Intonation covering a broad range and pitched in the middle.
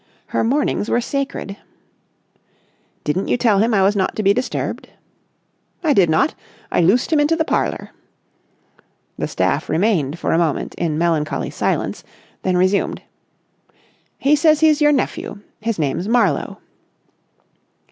No: wide, 7.9 semitones; high, 210 Hz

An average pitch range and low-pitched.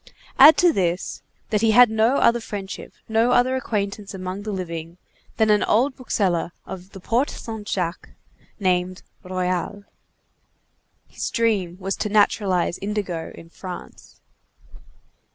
No: average, 3.5 semitones; high, 200 Hz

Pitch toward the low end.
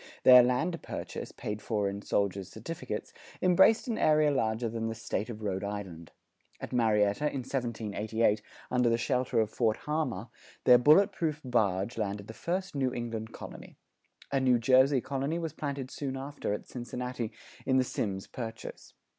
Yes: low, 120 Hz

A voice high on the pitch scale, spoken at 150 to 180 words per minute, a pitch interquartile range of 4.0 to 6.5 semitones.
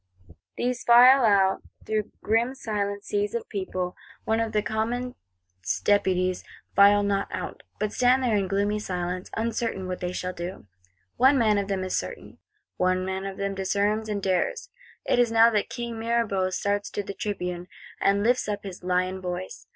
No: high, 205 Hz; average, 170 wpm; average, 3.3 semitones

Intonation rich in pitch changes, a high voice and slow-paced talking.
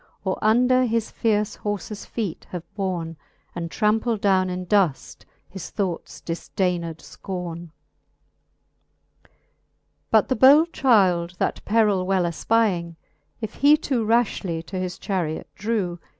No: average, 4.2 semitones; high, 195 Hz; slow, 125 wpm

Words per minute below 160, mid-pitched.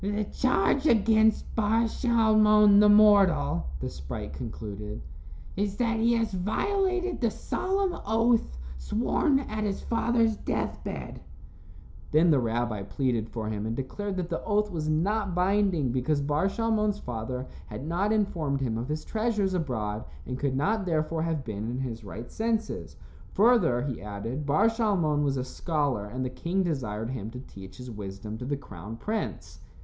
No: average, 165 wpm; medium, 160 Hz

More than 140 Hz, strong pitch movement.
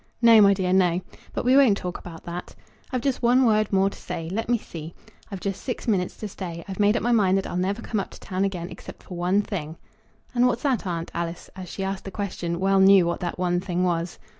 No: high, 190 Hz; average, 3.2 semitones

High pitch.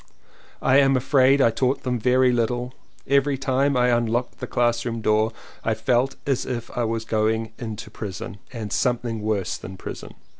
No: low, 120 Hz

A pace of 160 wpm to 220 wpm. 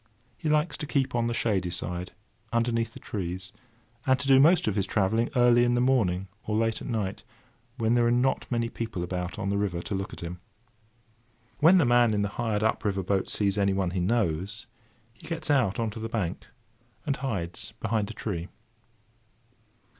Yes: average, 195 wpm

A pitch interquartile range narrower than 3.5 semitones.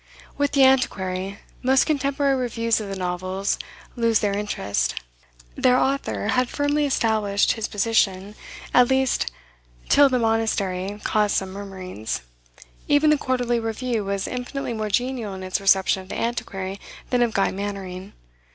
No: average, 4.5 semitones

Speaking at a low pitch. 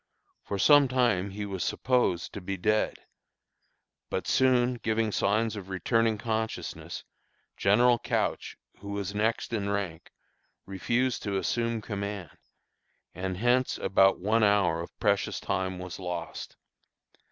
Yes: low, 105 Hz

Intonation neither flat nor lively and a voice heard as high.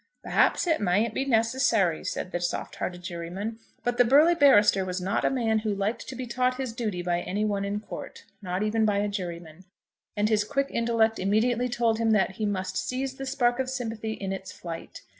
Yes: average, 4.2 semitones; high, 215 Hz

